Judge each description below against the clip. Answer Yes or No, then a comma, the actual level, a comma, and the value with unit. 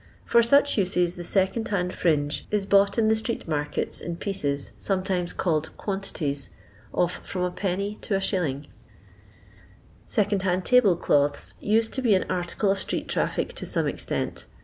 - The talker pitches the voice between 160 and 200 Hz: Yes, high, 190 Hz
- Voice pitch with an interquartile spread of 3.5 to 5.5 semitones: No, average, 3.1 semitones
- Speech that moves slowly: No, average, 150 wpm